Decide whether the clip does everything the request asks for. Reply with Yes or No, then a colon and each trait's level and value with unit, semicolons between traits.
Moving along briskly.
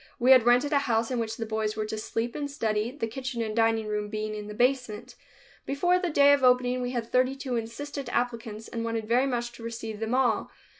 Yes: fast, 235 wpm